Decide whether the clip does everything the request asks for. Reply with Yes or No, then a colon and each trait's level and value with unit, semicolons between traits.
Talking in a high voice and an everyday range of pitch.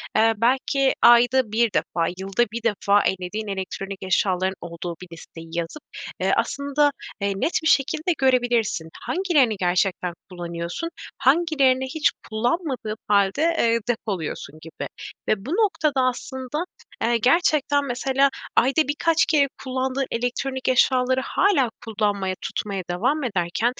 No: high, 240 Hz; wide, 5.9 semitones